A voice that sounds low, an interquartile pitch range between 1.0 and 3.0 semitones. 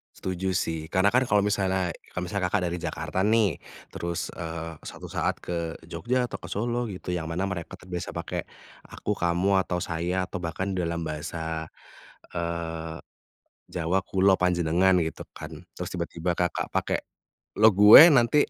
Yes: very low, 90 Hz; narrow, 2.6 semitones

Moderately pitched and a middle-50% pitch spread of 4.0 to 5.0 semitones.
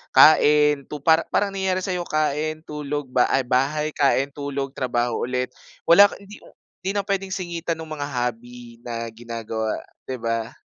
Yes: medium, 145 Hz; average, 4.7 semitones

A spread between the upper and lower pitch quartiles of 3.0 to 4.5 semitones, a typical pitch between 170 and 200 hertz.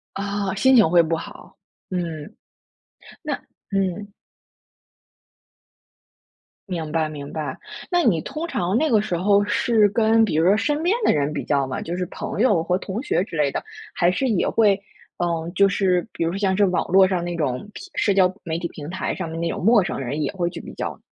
Yes: average, 3.9 semitones; medium, 185 Hz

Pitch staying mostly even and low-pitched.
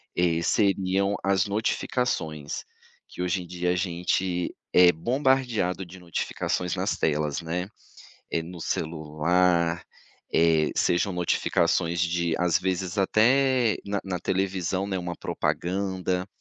Yes: narrow, 2.3 semitones; very low, 90 Hz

